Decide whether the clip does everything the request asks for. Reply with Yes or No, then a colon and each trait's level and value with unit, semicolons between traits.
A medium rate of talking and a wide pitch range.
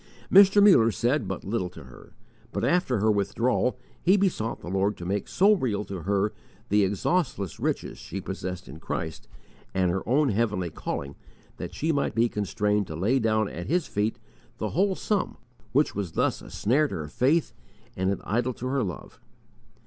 Yes: average, 185 wpm; wide, 6.3 semitones